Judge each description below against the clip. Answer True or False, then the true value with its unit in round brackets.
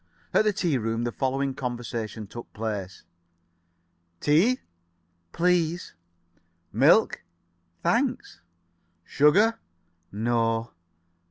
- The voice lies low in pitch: True (125 Hz)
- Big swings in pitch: True (6.9 semitones)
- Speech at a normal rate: False (85 wpm)